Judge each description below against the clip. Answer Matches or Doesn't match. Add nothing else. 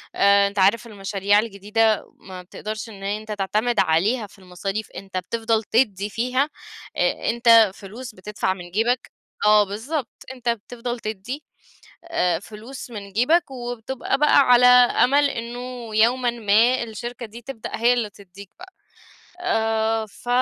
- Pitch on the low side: Doesn't match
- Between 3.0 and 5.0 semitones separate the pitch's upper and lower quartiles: Matches